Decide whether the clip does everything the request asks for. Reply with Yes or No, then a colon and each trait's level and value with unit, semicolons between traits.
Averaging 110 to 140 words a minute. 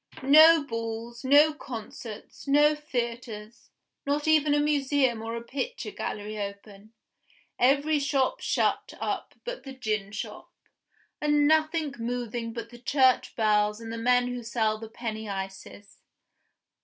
Yes: slow, 135 wpm